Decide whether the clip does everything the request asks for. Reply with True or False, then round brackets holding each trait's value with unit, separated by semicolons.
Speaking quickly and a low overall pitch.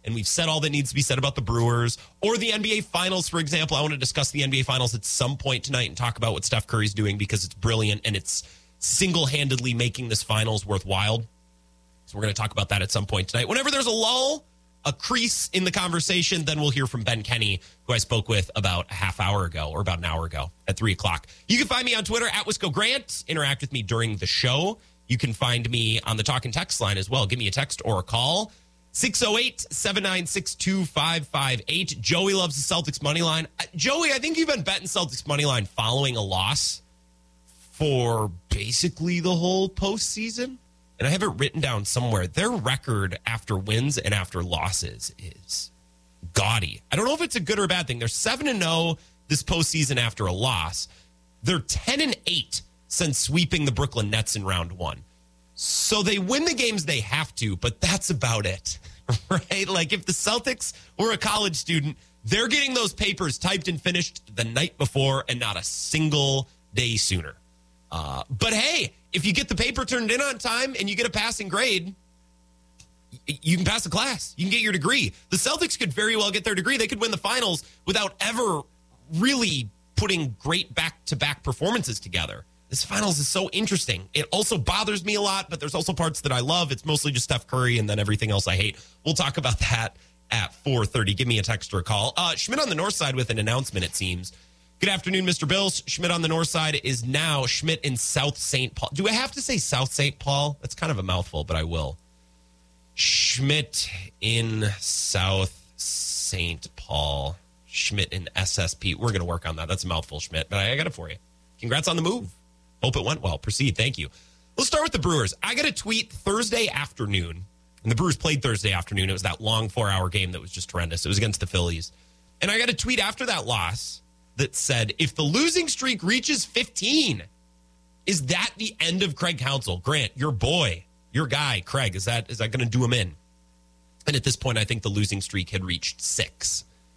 True (210 wpm; 125 Hz)